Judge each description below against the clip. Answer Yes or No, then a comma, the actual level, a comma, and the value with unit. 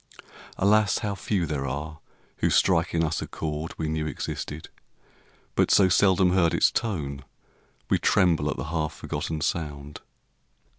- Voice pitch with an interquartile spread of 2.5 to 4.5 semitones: Yes, average, 3.5 semitones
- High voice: No, very low, 80 Hz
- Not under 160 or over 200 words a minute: No, average, 150 wpm